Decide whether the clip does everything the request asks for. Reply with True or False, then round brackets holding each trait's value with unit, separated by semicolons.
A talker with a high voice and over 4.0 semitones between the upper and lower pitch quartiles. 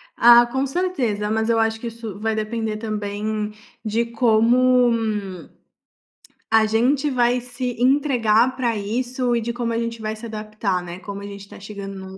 False (225 Hz; 2.4 semitones)